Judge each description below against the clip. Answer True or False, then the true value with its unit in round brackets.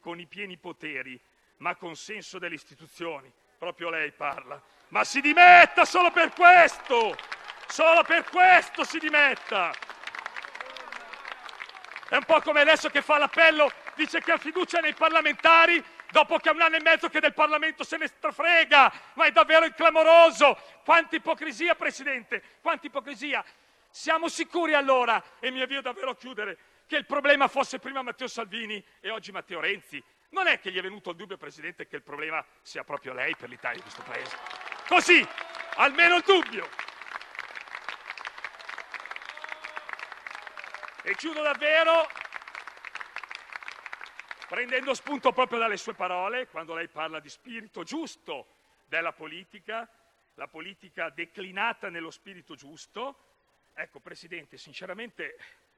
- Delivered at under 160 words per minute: True (140 wpm)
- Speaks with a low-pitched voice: False (285 Hz)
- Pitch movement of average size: False (7.9 semitones)